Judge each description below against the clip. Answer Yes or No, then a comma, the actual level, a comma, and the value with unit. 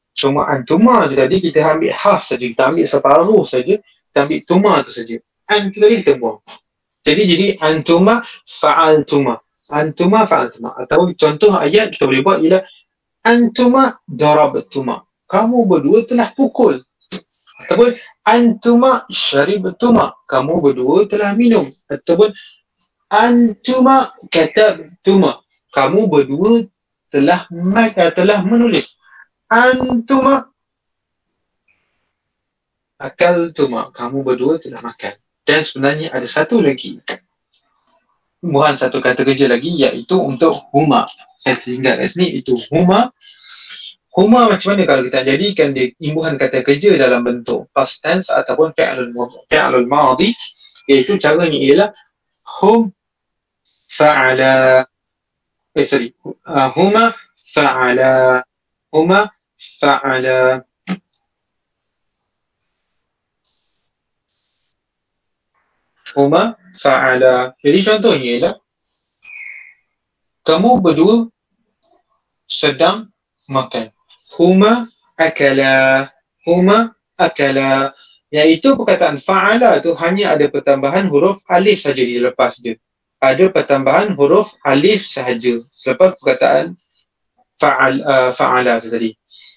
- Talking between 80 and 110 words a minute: Yes, average, 100 wpm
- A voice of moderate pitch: Yes, medium, 170 Hz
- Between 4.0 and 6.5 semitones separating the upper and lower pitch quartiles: No, wide, 7.9 semitones